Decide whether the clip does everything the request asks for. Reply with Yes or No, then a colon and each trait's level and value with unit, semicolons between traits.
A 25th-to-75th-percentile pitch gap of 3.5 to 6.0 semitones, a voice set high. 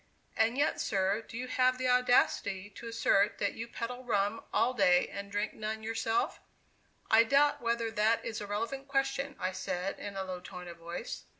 Yes: average, 3.8 semitones; high, 225 Hz